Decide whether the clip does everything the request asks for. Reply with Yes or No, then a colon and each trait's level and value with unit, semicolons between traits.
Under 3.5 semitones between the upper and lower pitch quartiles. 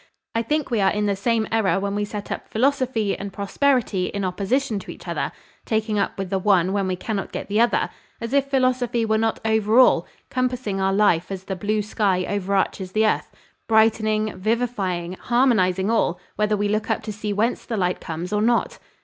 Yes: average, 2.9 semitones